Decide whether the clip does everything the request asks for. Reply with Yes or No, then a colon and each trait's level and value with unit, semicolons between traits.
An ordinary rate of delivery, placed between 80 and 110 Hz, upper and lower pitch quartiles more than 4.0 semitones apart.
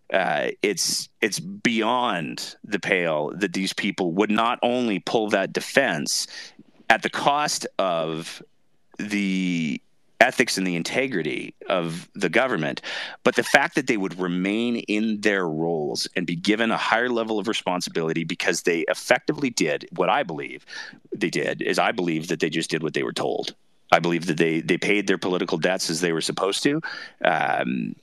Yes: average, 170 wpm; very low, 95 Hz; average, 4.4 semitones